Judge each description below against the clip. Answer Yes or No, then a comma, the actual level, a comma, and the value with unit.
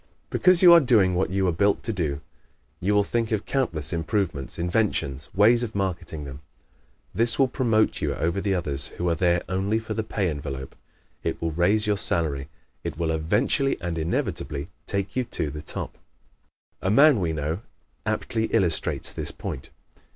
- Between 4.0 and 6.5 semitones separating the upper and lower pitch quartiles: Yes, average, 5.2 semitones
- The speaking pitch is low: Yes, very low, 95 Hz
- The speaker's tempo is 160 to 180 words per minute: Yes, average, 175 wpm